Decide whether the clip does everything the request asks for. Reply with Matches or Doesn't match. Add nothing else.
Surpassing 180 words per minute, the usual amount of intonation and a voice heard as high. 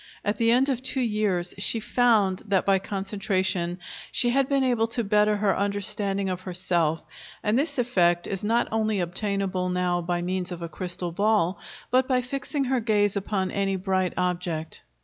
Doesn't match